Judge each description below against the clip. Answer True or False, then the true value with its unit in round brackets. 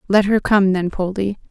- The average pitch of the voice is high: True (195 Hz)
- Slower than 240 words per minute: True (200 wpm)